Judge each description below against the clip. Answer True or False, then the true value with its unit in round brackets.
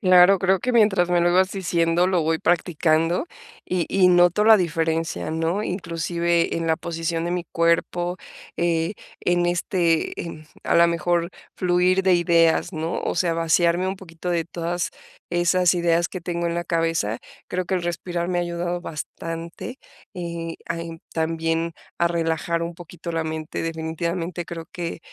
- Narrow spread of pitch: True (1.3 semitones)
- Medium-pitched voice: True (170 Hz)